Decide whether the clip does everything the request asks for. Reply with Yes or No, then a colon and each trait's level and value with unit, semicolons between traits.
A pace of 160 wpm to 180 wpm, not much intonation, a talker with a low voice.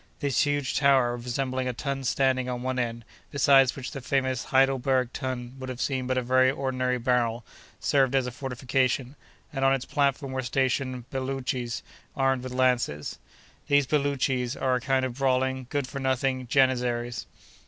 Yes: average, 165 wpm; narrow, 1.3 semitones; low, 130 Hz